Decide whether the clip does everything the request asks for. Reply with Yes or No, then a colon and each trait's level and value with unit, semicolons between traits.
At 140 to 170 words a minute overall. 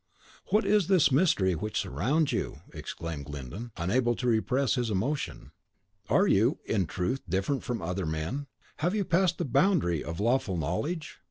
Yes: average, 160 wpm